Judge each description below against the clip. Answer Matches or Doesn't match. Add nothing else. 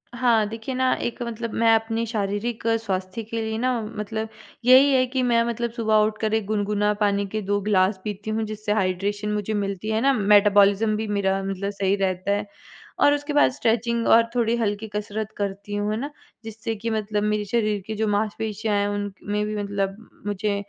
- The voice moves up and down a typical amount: Doesn't match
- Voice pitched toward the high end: Matches